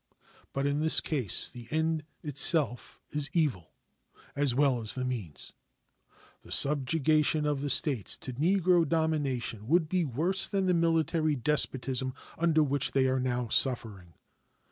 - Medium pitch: Yes, medium, 145 Hz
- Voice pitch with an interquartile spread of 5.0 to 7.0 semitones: No, average, 3.9 semitones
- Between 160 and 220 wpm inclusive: No, average, 145 wpm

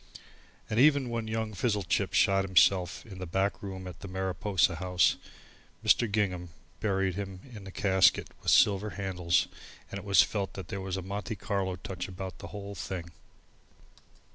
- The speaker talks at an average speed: Yes, average, 165 wpm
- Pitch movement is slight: Yes, narrow, 1.8 semitones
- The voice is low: Yes, very low, 95 Hz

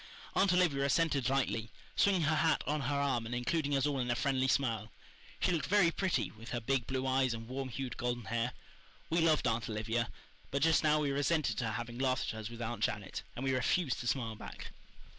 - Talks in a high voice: No, low, 130 Hz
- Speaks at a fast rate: Yes, fast, 215 wpm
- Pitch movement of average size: Yes, average, 4.0 semitones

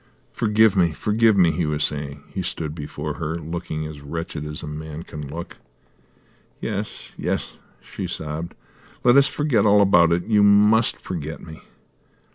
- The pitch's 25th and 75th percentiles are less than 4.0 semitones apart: No, average, 5.2 semitones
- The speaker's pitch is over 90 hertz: No, very low, 85 Hz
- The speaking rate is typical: Yes, average, 160 wpm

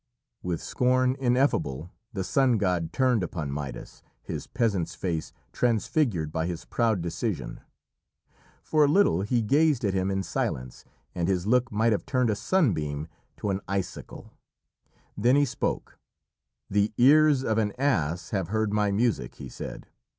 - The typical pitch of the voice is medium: No, low, 105 Hz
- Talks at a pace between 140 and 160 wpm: Yes, average, 150 wpm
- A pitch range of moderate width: No, wide, 6.3 semitones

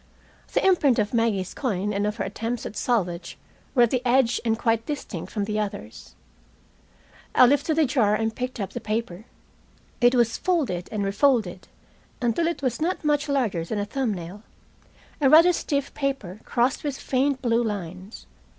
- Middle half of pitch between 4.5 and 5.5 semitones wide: Yes, average, 4.8 semitones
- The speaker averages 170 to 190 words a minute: Yes, average, 175 wpm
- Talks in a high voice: Yes, high, 230 Hz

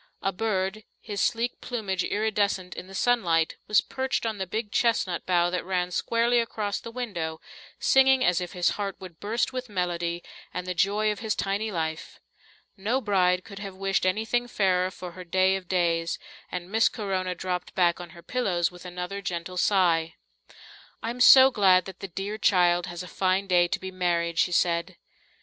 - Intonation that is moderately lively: Yes, average, 3.1 semitones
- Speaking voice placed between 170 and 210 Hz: Yes, medium, 185 Hz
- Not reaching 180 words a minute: No, average, 185 wpm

